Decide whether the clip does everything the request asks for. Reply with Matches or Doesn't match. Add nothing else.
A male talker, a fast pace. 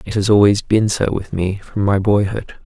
Matches